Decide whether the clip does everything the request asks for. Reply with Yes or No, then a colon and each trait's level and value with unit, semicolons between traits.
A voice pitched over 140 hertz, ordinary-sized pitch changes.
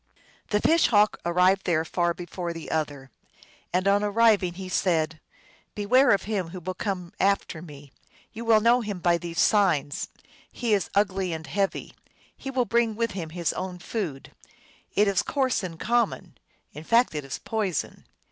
Yes: high, 190 Hz; average, 4.0 semitones